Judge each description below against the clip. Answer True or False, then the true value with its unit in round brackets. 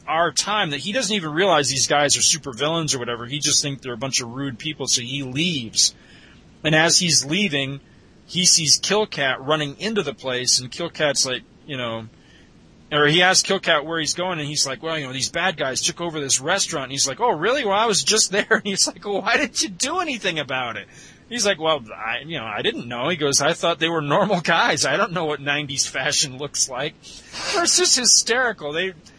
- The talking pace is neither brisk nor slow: False (235 wpm)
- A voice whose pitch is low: False (155 Hz)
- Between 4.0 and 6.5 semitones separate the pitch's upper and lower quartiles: True (5.5 semitones)